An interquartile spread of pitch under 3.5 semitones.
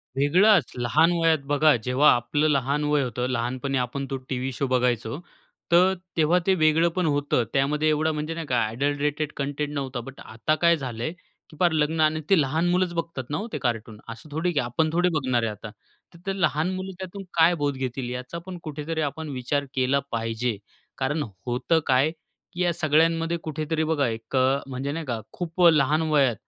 No: average, 4.0 semitones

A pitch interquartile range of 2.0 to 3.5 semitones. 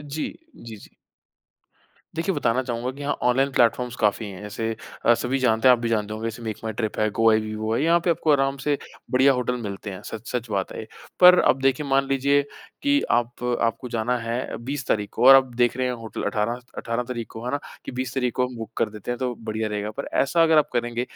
Yes: average, 3.2 semitones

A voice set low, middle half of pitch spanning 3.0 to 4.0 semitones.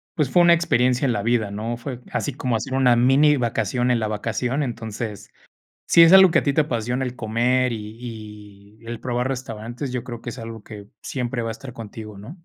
No: low, 120 Hz; narrow, 2.6 semitones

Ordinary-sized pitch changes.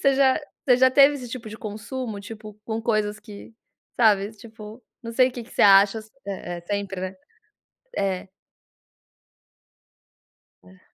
Yes: average, 3.3 semitones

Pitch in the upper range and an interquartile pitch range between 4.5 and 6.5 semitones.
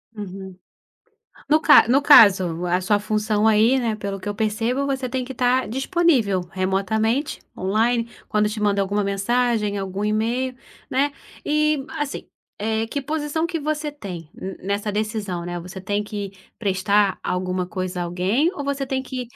Yes: high, 215 Hz; average, 5.0 semitones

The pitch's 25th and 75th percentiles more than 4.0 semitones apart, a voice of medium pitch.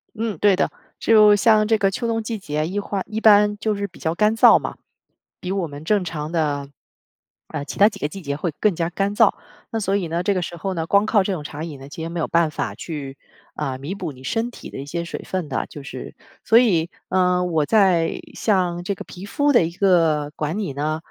Yes: average, 4.7 semitones; medium, 180 Hz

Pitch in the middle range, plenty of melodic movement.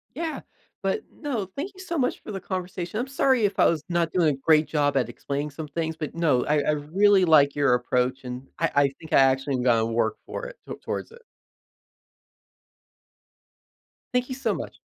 Yes: medium, 160 Hz; wide, 6.9 semitones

